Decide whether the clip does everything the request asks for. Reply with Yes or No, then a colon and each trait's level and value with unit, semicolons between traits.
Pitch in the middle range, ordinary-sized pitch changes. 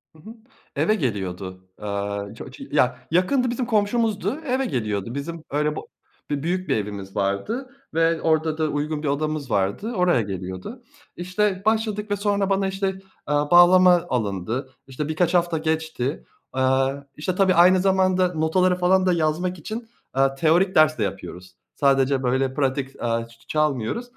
No: medium, 155 Hz; wide, 6.2 semitones